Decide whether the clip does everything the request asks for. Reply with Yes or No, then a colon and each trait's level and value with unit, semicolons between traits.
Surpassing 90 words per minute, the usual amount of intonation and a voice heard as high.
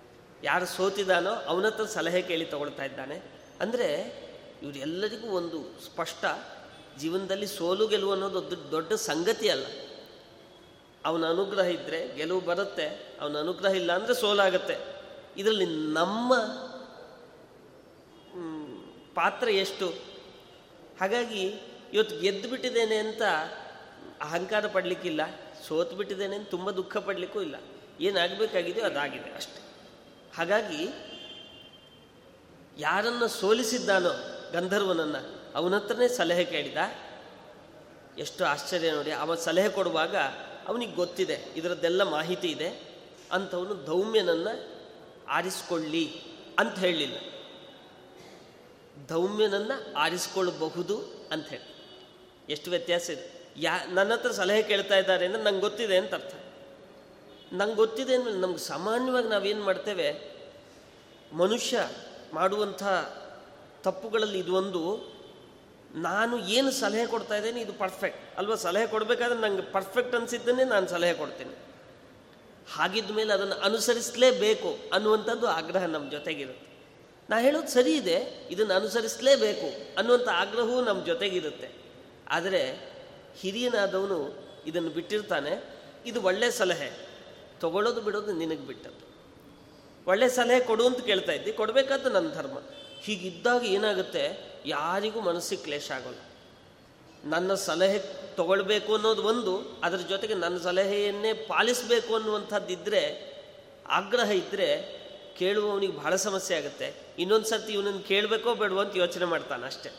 Yes: average, 100 wpm; average, 4.0 semitones; high, 200 Hz